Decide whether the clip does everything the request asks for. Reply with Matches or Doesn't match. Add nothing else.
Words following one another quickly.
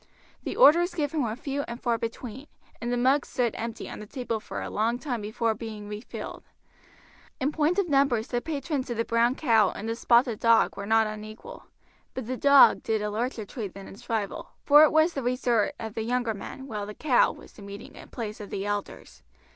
Matches